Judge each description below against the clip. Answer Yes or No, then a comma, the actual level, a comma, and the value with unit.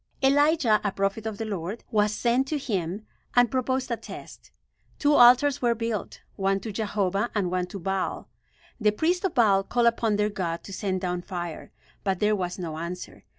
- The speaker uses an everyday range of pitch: Yes, average, 4.1 semitones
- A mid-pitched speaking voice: No, high, 210 Hz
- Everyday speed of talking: Yes, average, 190 wpm